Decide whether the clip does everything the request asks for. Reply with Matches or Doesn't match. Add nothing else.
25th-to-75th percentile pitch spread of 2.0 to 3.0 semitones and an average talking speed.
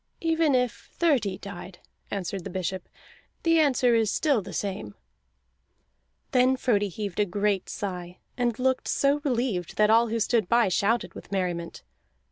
Doesn't match